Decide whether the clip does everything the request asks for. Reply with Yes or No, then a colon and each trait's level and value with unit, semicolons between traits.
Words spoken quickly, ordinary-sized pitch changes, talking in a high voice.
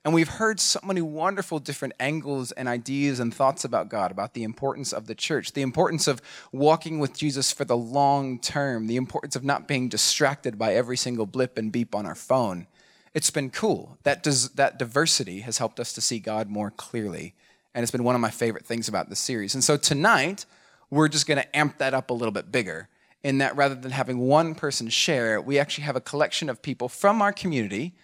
No: fast, 220 wpm; average, 3.8 semitones; low, 135 Hz